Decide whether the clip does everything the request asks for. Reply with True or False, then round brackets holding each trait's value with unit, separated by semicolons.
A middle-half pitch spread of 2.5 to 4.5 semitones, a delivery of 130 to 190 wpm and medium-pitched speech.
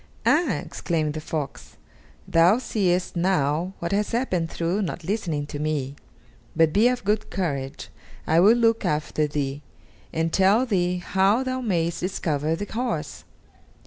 False (5.1 semitones; 145 wpm; 175 Hz)